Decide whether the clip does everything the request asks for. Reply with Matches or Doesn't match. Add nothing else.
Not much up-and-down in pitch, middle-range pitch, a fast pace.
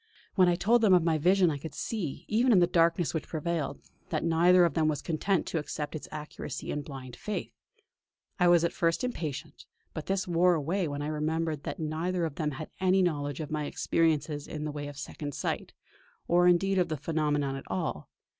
Doesn't match